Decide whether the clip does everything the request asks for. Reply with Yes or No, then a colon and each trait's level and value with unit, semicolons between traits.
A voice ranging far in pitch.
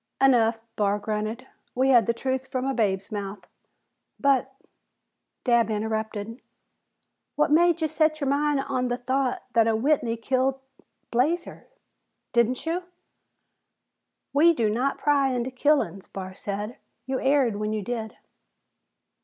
No: average, 3.9 semitones